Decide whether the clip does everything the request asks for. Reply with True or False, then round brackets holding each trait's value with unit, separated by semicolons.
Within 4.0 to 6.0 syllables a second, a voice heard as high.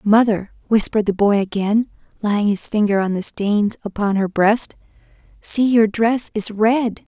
True (4.3 syllables/s; 210 Hz)